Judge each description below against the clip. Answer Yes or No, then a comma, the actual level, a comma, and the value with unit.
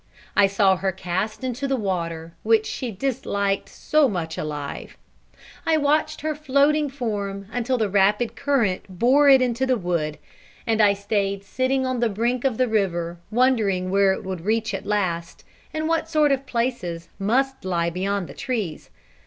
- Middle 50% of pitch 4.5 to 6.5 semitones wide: Yes, wide, 5.4 semitones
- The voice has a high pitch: Yes, high, 215 Hz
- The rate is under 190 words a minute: Yes, average, 170 wpm